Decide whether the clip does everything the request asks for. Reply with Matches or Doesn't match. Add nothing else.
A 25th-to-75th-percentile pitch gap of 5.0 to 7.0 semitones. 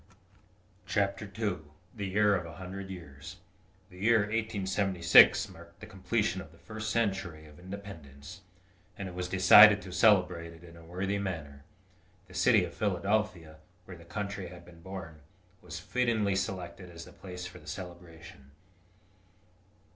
Doesn't match